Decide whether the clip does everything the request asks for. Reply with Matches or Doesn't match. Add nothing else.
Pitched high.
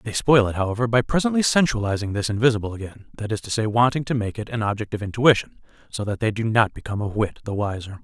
Doesn't match